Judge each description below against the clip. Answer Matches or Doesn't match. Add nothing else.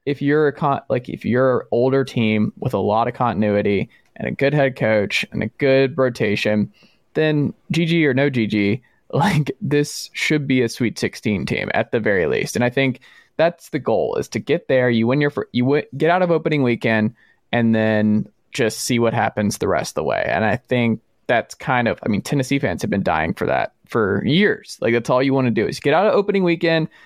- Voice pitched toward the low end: Matches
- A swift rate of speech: Matches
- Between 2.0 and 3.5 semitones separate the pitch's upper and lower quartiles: Doesn't match